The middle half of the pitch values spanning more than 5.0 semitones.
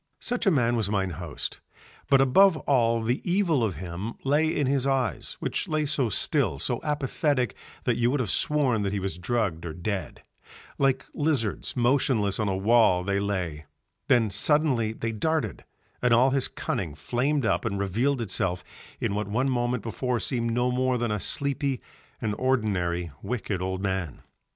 Yes: wide, 5.4 semitones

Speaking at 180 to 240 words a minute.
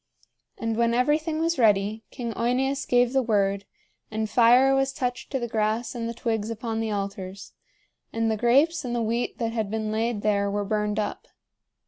Yes: average, 185 wpm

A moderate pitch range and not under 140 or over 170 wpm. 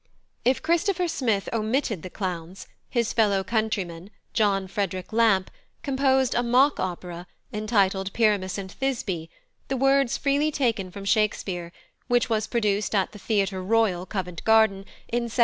Yes: average, 4.2 semitones; average, 145 wpm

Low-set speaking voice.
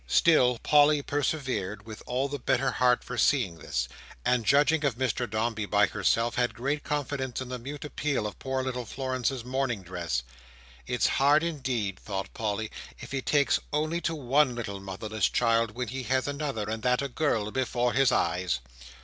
Yes: low, 125 Hz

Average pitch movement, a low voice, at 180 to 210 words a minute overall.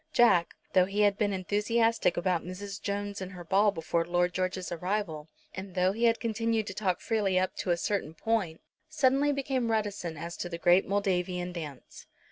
No: average, 3.2 semitones; high, 190 Hz; average, 185 wpm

